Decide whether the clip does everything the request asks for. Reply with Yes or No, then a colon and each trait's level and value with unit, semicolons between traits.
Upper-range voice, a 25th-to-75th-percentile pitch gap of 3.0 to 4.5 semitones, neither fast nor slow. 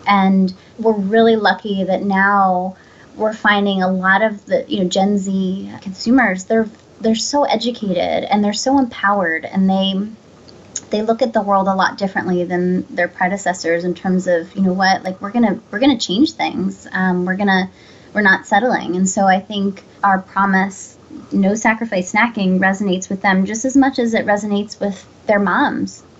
No: high, 195 Hz; narrow, 2.5 semitones; average, 180 wpm